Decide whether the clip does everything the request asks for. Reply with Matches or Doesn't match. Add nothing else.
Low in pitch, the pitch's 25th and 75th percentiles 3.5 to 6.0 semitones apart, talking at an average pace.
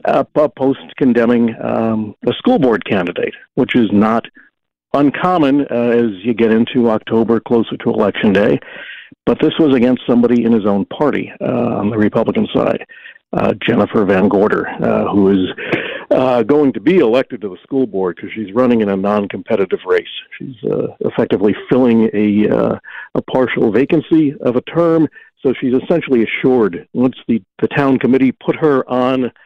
Matches